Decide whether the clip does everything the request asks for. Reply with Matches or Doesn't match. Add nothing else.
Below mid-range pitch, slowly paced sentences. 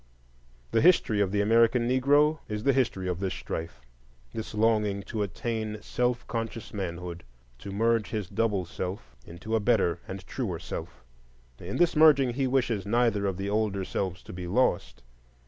Doesn't match